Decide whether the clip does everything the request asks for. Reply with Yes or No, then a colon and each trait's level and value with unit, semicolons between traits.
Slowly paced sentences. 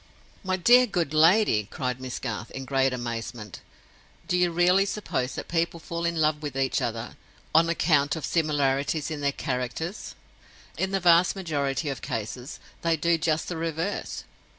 No: average, 165 wpm